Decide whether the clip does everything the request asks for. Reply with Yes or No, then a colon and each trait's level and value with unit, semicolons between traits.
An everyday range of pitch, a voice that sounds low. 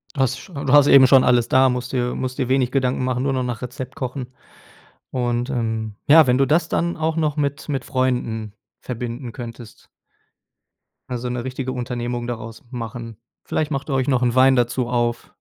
No: narrow, 1.9 semitones; low, 125 Hz